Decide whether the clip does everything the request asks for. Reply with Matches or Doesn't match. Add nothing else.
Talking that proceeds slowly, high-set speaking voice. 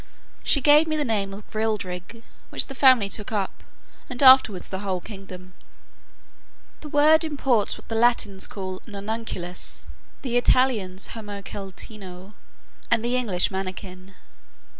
Matches